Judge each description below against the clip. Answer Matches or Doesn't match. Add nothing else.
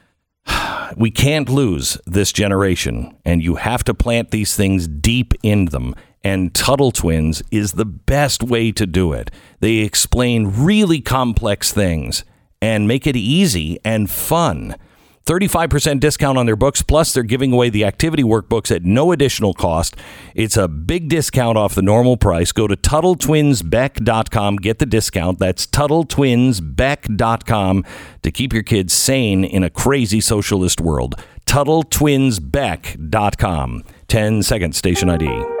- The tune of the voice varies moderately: Doesn't match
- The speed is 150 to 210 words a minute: Doesn't match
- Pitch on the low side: Matches